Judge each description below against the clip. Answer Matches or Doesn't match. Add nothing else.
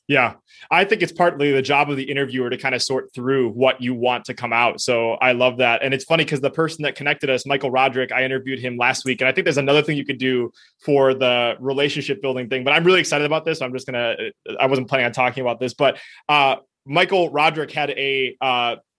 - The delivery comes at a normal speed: Doesn't match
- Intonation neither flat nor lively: Doesn't match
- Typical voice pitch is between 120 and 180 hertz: Matches